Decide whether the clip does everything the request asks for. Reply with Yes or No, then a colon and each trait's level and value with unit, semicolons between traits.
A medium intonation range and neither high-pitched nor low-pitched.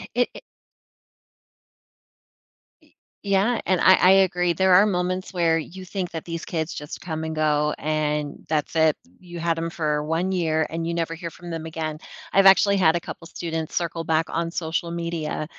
No: narrow, 2.1 semitones; medium, 165 Hz